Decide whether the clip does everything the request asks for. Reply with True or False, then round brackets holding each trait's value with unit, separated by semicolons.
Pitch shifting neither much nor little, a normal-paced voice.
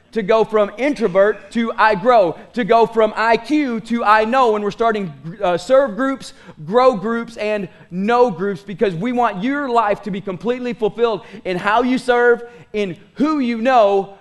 True (3.2 semitones; 175 wpm)